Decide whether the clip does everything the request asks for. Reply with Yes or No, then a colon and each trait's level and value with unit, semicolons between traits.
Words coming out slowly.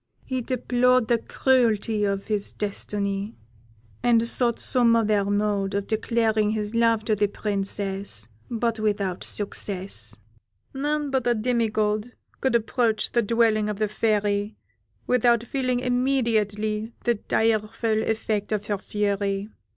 Yes: slow, 130 wpm